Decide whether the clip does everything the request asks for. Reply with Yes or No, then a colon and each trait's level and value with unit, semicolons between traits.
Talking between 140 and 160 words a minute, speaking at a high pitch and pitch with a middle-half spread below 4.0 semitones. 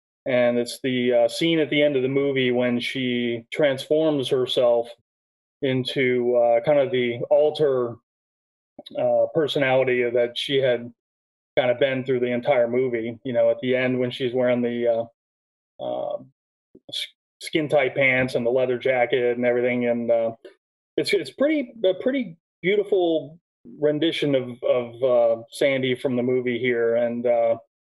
No: average, 155 wpm; low, 125 Hz; average, 3.3 semitones